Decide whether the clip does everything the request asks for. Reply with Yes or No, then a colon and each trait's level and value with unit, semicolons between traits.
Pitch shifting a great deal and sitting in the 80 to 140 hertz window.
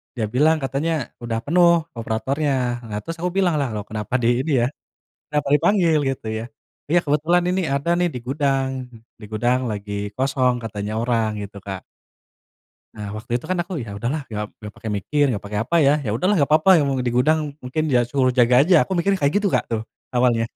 Yes: wide, 5.7 semitones; low, 135 Hz